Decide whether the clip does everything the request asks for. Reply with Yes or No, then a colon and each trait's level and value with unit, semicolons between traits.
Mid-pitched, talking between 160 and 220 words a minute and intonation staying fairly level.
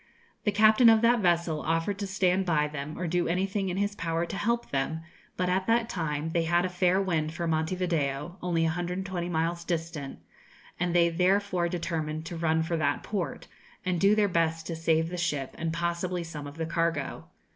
Yes: medium, 170 Hz; average, 200 wpm; narrow, 2.3 semitones